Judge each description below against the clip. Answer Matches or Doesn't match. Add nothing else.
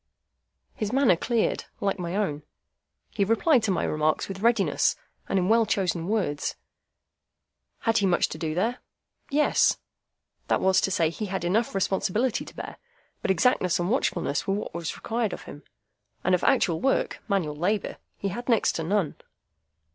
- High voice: Matches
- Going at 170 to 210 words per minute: Doesn't match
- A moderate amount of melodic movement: Matches